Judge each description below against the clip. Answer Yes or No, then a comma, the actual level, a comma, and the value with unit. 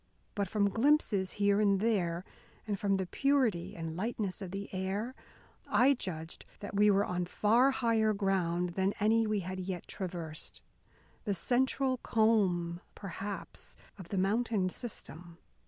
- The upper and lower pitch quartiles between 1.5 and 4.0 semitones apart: Yes, average, 3.3 semitones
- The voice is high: Yes, high, 200 Hz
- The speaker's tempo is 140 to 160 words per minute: Yes, average, 145 wpm